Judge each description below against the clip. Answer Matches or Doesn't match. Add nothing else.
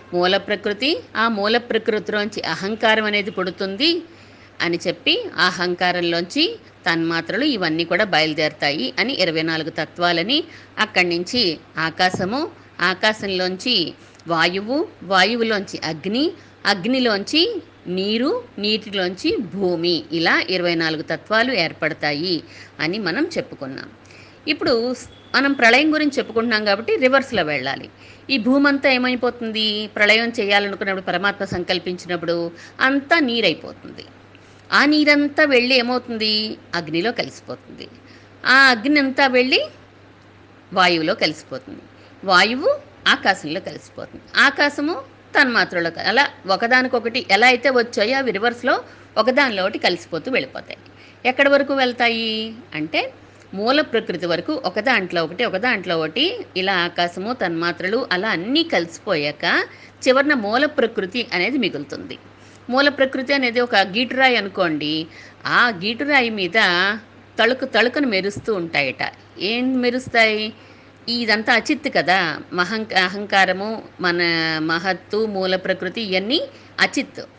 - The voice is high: Matches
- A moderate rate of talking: Matches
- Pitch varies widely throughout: Matches